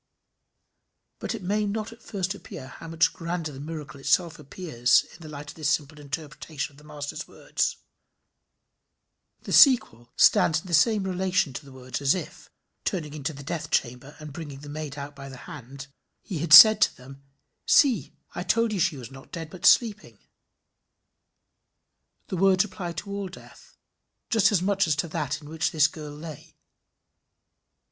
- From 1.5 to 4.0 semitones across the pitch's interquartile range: No, average, 4.6 semitones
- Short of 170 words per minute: No, average, 175 wpm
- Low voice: No, medium, 155 Hz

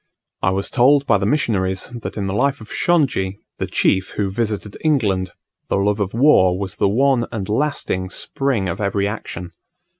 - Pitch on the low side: Yes, low, 105 Hz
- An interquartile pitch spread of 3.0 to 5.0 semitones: No, wide, 5.5 semitones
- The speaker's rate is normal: Yes, average, 180 wpm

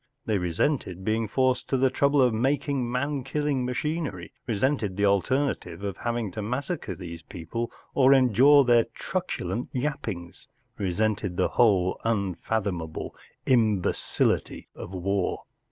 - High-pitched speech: No, low, 115 Hz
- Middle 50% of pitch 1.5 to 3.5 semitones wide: No, wide, 5.5 semitones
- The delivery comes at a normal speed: No, slow, 125 wpm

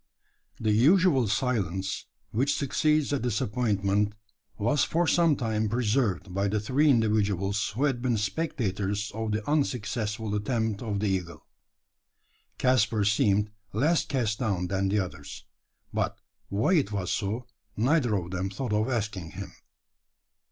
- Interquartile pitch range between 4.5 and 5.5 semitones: No, average, 4.0 semitones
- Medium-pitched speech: No, low, 110 Hz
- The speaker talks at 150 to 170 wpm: No, slow, 135 wpm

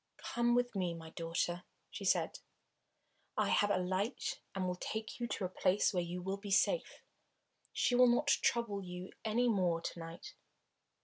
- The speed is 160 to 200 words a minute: Yes, average, 175 wpm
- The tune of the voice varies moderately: Yes, average, 4.8 semitones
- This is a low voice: No, high, 195 Hz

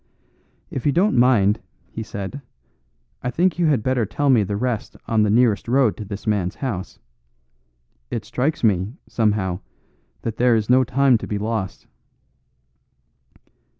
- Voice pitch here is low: Yes, low, 115 Hz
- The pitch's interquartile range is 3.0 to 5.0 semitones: Yes, average, 3.9 semitones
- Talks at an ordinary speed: Yes, average, 150 wpm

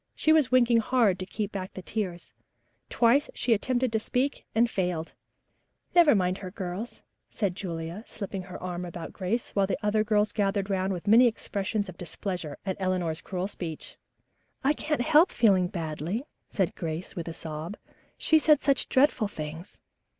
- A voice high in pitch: Yes, high, 195 Hz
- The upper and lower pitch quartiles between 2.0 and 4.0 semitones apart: No, average, 4.5 semitones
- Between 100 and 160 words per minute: No, average, 170 wpm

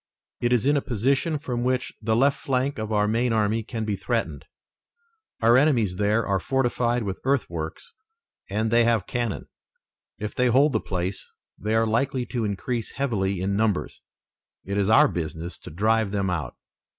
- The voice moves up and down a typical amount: Yes, average, 3.8 semitones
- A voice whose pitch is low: Yes, low, 110 Hz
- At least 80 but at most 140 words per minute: No, average, 175 wpm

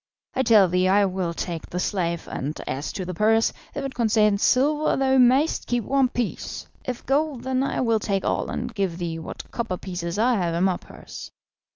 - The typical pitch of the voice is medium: No, high, 210 Hz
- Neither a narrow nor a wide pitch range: No, wide, 5.8 semitones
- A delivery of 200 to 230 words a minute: Yes, fast, 205 wpm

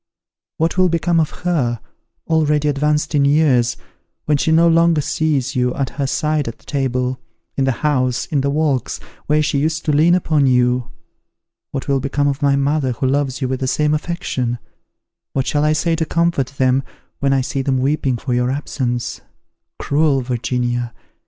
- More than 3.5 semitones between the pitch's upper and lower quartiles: No, average, 3.0 semitones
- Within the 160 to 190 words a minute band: Yes, average, 180 wpm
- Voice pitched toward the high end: No, medium, 140 Hz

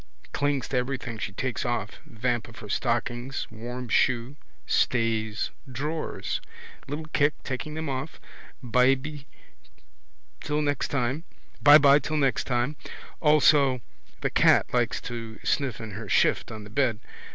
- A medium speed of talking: No, slow, 120 wpm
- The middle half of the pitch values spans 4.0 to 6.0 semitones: No, average, 3.5 semitones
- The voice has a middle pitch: No, low, 130 Hz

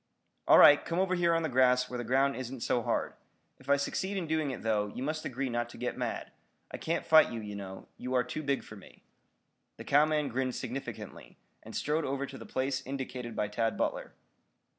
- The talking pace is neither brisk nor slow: No, fast, 220 wpm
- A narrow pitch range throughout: No, average, 3.7 semitones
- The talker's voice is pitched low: Yes, low, 130 Hz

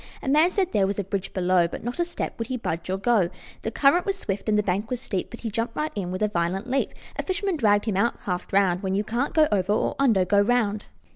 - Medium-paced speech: No, fast, 275 wpm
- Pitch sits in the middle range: No, high, 210 Hz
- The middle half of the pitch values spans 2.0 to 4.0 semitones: No, average, 4.7 semitones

